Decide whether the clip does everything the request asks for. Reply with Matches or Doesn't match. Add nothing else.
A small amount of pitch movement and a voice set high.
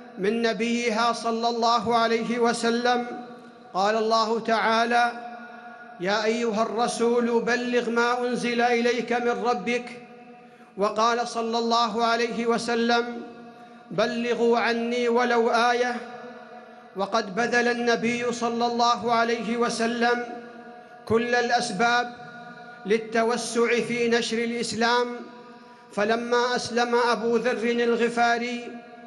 Matches